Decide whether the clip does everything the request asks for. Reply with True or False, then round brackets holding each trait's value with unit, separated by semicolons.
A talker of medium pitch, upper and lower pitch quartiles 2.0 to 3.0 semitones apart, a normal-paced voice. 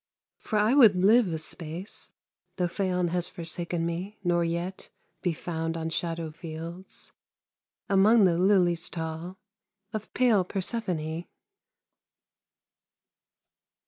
False (175 Hz; 2.7 semitones; 110 wpm)